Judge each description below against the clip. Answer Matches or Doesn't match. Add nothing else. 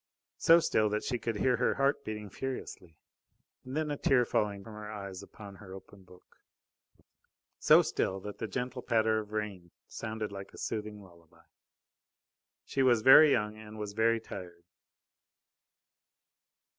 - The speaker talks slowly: Doesn't match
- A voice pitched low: Matches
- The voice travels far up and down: Doesn't match